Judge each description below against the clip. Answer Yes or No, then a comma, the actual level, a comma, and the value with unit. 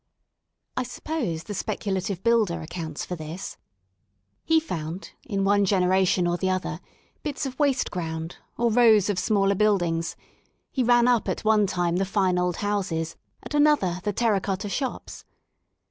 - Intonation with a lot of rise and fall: No, average, 4.3 semitones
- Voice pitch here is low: No, high, 195 Hz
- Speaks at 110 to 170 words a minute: Yes, average, 155 wpm